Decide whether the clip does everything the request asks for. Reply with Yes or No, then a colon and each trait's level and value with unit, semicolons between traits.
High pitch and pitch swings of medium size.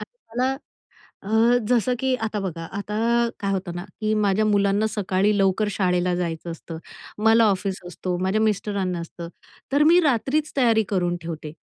Yes: high, 200 Hz; average, 3.4 semitones